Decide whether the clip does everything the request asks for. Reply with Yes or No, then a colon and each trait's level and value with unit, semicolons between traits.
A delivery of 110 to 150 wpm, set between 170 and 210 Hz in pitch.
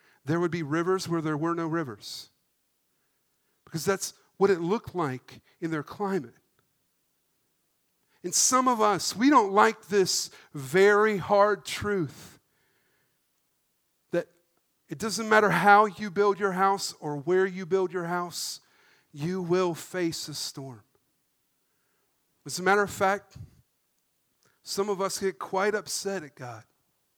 Yes: slow, 135 wpm; medium, 185 Hz